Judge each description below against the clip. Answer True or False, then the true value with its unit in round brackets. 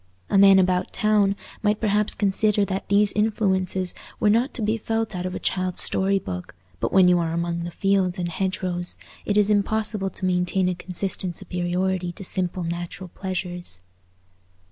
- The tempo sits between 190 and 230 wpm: False (170 wpm)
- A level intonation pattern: True (2.3 semitones)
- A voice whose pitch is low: False (190 Hz)